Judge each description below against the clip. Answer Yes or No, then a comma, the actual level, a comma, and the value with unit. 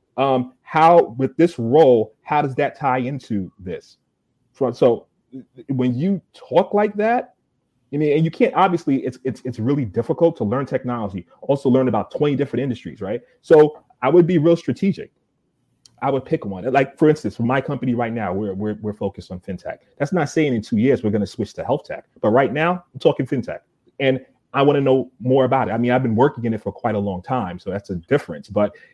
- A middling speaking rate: No, fast, 220 wpm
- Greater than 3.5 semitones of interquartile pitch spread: Yes, average, 4.2 semitones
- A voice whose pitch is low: Yes, low, 130 Hz